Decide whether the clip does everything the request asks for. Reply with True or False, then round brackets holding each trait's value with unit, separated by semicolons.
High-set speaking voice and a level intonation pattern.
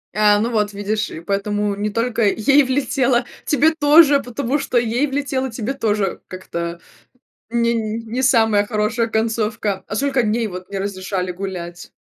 False (220 Hz; 3.7 semitones)